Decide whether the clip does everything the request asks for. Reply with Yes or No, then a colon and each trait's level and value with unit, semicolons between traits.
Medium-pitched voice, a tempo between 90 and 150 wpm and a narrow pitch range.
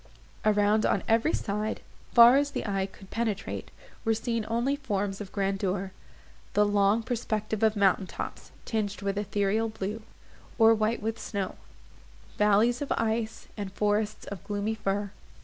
No: high, 210 Hz; average, 145 wpm; narrow, 1.9 semitones